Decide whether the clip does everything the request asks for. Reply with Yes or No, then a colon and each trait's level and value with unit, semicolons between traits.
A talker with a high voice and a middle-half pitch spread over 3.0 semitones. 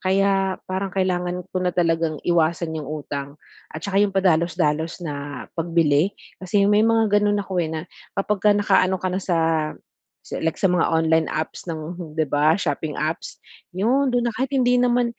No: medium, 180 Hz; average, 3.7 semitones